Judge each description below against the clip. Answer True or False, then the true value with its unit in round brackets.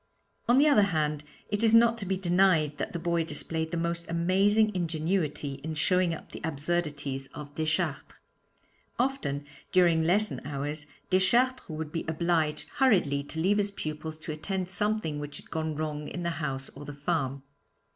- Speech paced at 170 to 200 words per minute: True (175 wpm)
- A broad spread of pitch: False (4.0 semitones)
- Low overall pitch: False (165 Hz)